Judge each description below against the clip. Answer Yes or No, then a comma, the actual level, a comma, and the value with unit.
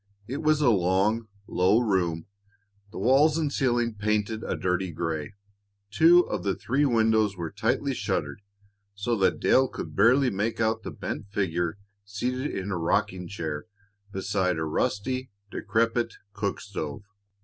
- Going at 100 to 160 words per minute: Yes, average, 150 wpm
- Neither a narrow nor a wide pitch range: Yes, average, 4.3 semitones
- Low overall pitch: Yes, low, 105 Hz